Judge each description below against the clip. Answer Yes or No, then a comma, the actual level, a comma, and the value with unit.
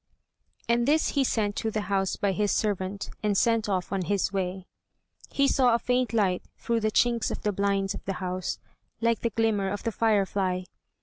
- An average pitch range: Yes, average, 3.0 semitones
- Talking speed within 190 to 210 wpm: Yes, average, 195 wpm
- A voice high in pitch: Yes, high, 205 Hz